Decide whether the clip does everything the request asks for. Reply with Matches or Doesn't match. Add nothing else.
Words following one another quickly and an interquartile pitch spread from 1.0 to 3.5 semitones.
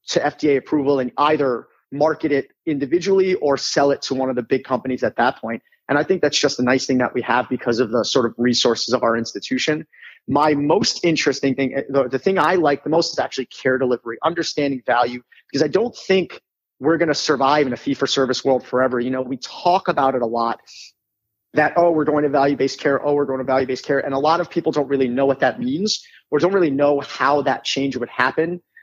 Matches